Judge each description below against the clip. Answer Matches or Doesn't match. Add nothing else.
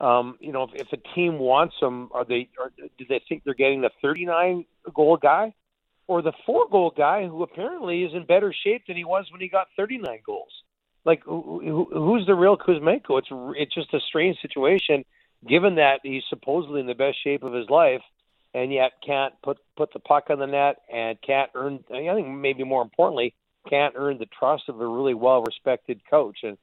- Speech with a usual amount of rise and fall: Matches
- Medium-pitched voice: Matches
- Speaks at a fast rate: Matches